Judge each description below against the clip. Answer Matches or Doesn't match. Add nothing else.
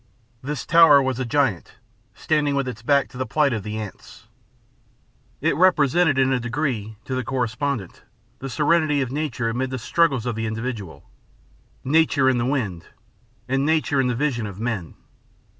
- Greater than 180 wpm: Doesn't match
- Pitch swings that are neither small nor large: Matches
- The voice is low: Matches